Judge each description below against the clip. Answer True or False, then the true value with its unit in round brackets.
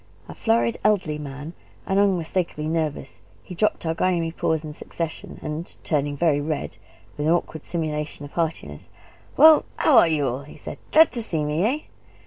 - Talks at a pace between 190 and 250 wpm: False (175 wpm)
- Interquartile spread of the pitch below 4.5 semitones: True (3.1 semitones)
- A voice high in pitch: False (160 Hz)